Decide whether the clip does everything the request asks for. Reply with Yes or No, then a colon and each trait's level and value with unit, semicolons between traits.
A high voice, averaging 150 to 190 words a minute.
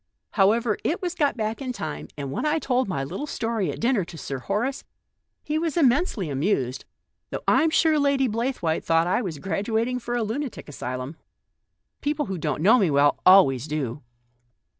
Yes: high, 215 Hz; average, 180 wpm